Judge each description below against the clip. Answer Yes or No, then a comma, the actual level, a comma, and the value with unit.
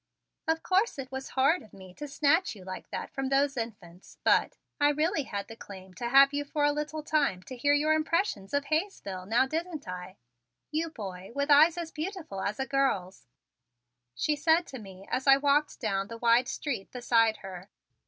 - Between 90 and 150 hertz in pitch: No, very high, 275 Hz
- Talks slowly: No, average, 195 wpm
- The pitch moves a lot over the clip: Yes, wide, 7.0 semitones